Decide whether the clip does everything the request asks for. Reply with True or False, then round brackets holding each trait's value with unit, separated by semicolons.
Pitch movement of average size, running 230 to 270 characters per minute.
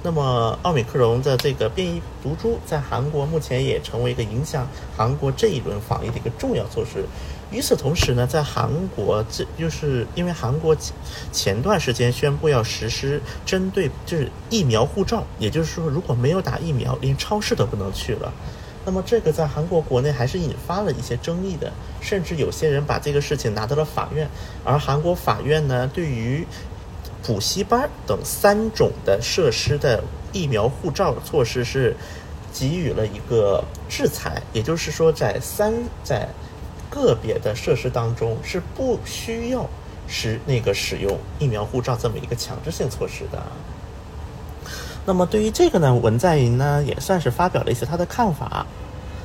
False (5.8 semitones; 265 characters per minute)